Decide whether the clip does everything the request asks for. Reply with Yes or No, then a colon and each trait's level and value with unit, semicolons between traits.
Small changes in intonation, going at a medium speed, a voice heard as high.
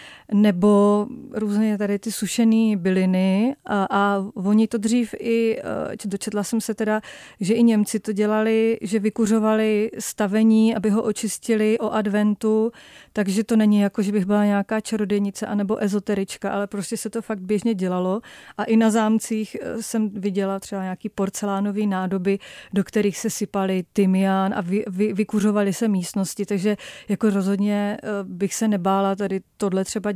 Yes: narrow, 1.7 semitones; average, 155 wpm; high, 210 Hz